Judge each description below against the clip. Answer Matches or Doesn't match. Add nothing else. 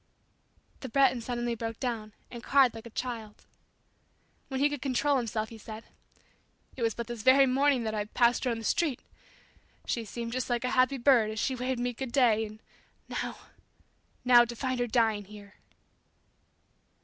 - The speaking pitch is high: Matches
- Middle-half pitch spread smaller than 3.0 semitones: Matches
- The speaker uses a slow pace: Doesn't match